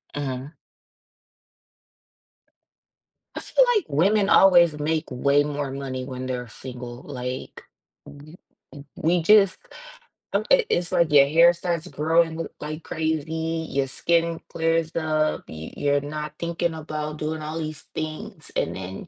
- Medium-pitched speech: Yes, medium, 155 Hz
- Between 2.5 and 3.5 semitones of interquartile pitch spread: Yes, average, 2.8 semitones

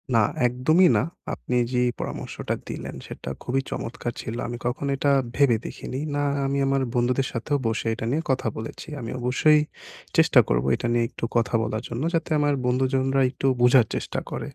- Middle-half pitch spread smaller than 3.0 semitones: Yes, narrow, 2.6 semitones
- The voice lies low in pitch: Yes, low, 125 Hz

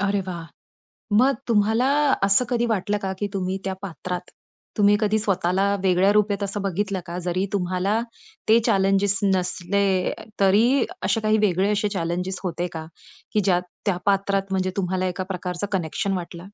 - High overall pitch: Yes, high, 195 Hz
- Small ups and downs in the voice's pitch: Yes, narrow, 2.1 semitones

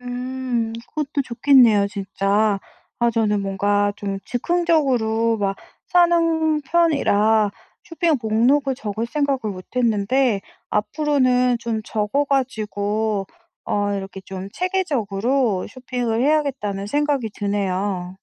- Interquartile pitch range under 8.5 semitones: Yes, average, 5.3 semitones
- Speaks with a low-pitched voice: No, high, 230 Hz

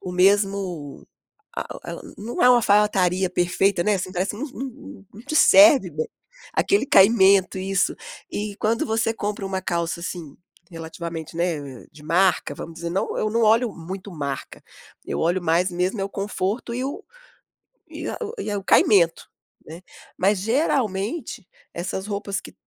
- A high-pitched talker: Yes, high, 195 Hz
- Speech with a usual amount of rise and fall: Yes, average, 3.6 semitones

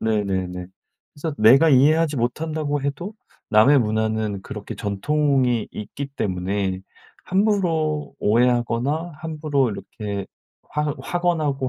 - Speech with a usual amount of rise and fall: No, wide, 6.2 semitones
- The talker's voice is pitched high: No, low, 135 Hz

